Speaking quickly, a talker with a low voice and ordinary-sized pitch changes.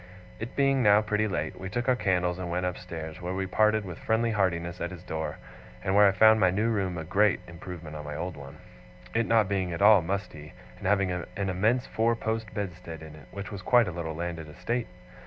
Yes: fast, 225 wpm; very low, 95 Hz; average, 3.9 semitones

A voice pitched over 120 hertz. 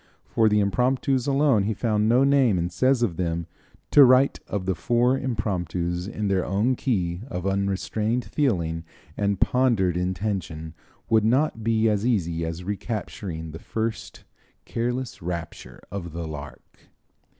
No: low, 105 Hz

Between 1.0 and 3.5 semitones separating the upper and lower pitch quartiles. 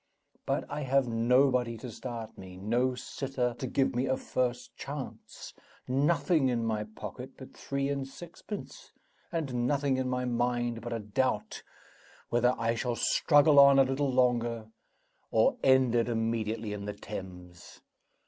Yes: average, 2.8 semitones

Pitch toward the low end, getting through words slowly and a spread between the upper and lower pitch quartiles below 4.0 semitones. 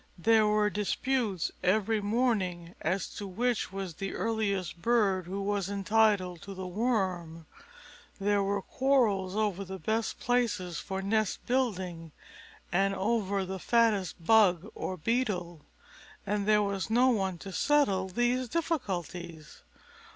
No: high, 200 Hz; slow, 130 wpm; average, 3.2 semitones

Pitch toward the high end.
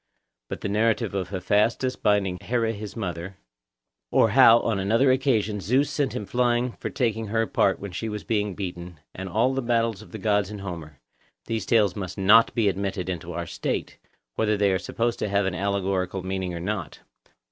No: low, 105 Hz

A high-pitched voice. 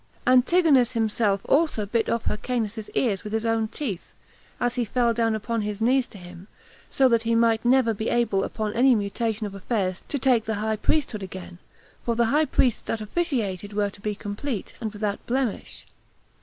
Yes: high, 225 Hz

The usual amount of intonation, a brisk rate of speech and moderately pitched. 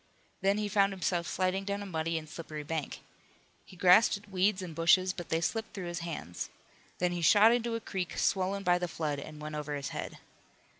Yes: average, 3.4 semitones; fast, 210 wpm; medium, 180 Hz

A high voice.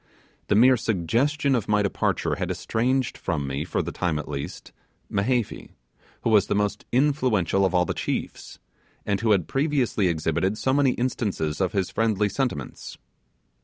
No: low, 105 Hz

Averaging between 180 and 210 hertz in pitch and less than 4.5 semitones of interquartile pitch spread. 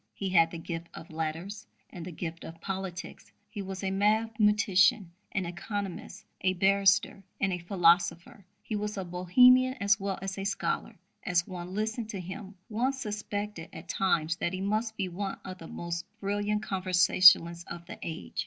Yes: high, 190 Hz; average, 3.0 semitones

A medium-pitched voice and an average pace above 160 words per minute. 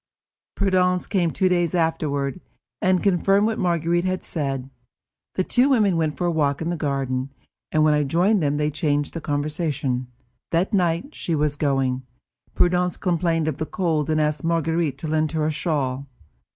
Yes: medium, 160 Hz; average, 180 wpm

